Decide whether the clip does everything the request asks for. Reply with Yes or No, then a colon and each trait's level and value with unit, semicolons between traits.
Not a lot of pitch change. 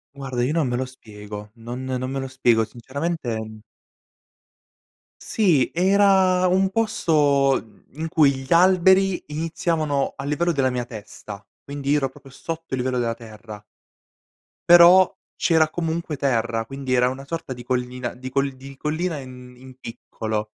No: average, 4.9 semitones